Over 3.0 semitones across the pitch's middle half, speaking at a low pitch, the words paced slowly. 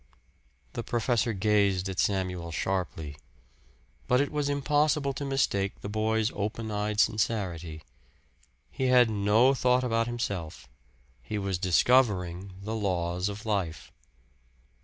Yes: average, 4.4 semitones; low, 105 Hz; slow, 120 wpm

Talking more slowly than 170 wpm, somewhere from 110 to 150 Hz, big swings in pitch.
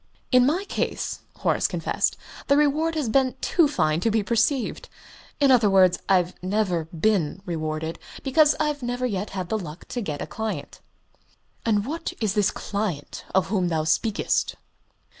No: average, 160 wpm; high, 215 Hz; wide, 6.5 semitones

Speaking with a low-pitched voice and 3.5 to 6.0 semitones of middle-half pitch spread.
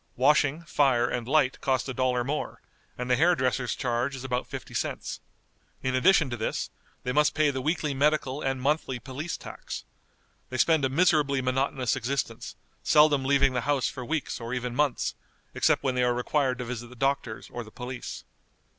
No: low, 130 Hz; narrow, 2.6 semitones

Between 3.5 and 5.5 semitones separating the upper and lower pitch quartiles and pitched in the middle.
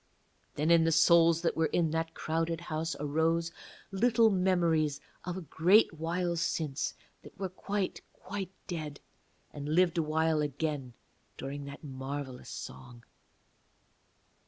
No: average, 2.7 semitones; medium, 165 Hz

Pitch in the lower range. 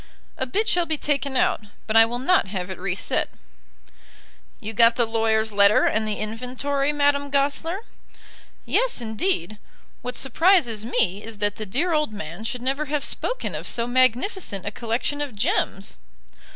No: high, 245 Hz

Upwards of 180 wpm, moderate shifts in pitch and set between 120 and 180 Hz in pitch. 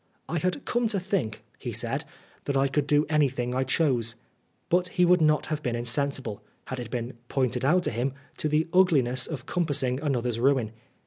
Yes: average, 200 wpm; average, 4.3 semitones; medium, 140 Hz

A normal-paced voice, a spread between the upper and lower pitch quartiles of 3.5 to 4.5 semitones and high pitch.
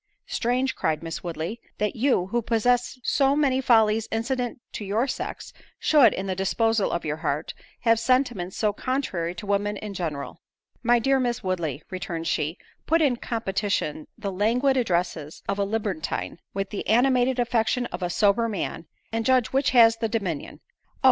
No: average, 170 wpm; average, 4.9 semitones; high, 220 Hz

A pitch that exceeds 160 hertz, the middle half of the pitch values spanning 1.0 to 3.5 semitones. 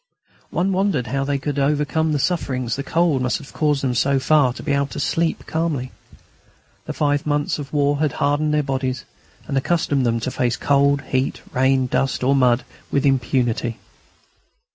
No: medium, 140 Hz; narrow, 2.4 semitones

